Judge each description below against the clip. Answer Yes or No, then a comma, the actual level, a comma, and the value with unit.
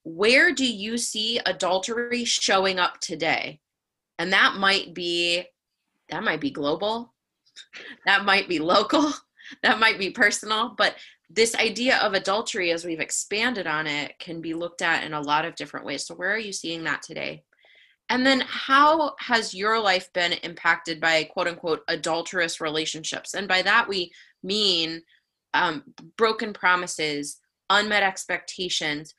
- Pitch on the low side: No, medium, 185 Hz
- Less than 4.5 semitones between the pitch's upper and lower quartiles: No, average, 5.1 semitones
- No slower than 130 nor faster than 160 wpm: Yes, average, 150 wpm